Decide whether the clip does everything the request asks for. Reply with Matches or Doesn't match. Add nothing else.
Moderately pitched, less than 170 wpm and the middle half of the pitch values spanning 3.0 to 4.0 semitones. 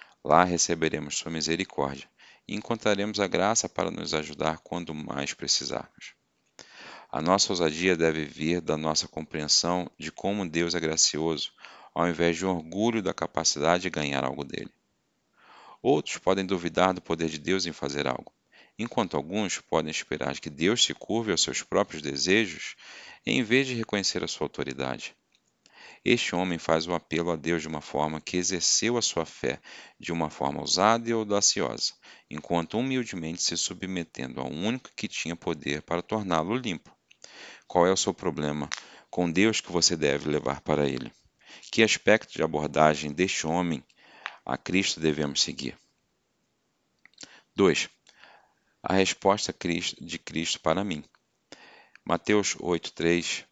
Doesn't match